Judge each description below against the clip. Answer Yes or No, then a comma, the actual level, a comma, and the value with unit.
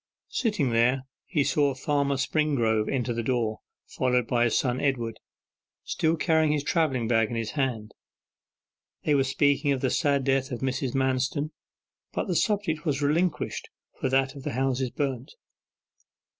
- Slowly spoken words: No, average, 155 wpm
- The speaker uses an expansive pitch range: No, average, 3.0 semitones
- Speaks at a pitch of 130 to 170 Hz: Yes, low, 135 Hz